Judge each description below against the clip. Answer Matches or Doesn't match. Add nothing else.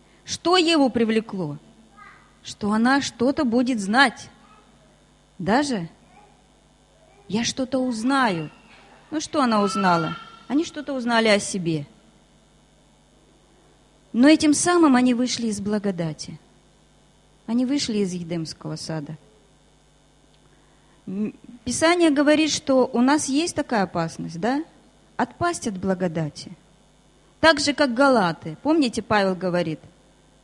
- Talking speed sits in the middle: Doesn't match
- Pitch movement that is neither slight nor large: Doesn't match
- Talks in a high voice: Matches